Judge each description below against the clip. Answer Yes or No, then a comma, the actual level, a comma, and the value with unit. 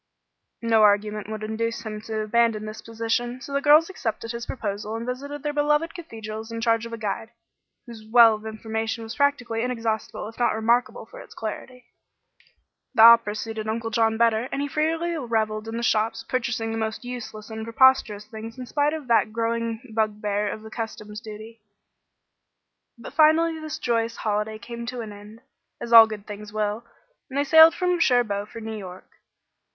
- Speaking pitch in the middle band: No, high, 225 Hz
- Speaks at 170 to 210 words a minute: Yes, average, 180 wpm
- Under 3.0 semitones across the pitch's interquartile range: Yes, narrow, 2.4 semitones